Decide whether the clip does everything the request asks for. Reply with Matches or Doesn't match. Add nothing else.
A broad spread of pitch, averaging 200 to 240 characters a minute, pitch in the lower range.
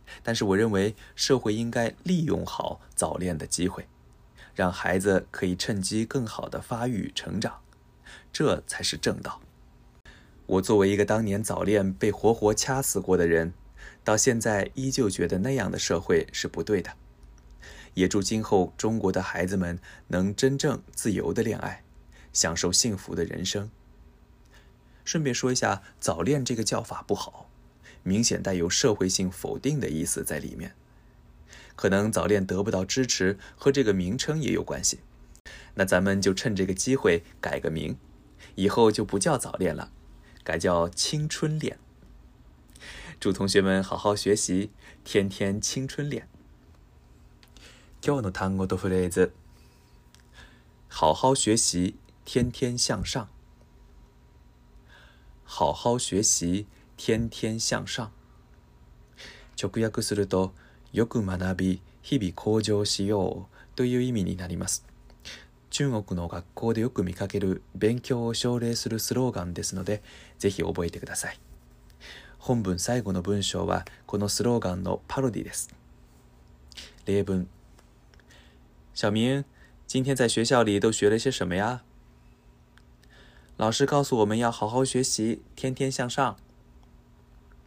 Matches